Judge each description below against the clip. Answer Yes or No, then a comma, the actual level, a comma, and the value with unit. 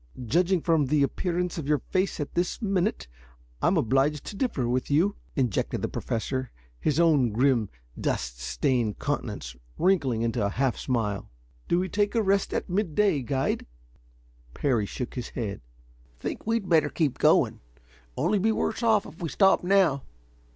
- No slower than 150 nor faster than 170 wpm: Yes, average, 160 wpm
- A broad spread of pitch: Yes, wide, 7.2 semitones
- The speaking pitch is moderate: Yes, medium, 150 Hz